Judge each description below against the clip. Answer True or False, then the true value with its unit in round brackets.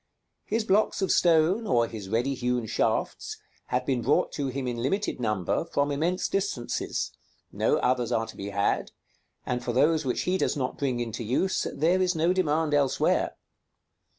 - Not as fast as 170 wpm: False (175 wpm)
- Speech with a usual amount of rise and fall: False (5.9 semitones)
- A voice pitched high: False (140 Hz)